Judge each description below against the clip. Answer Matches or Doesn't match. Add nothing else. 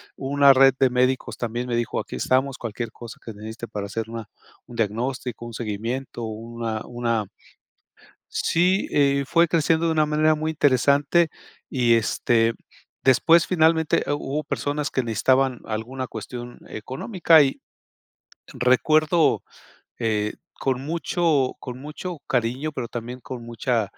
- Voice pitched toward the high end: Doesn't match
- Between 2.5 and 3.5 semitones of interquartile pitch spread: Doesn't match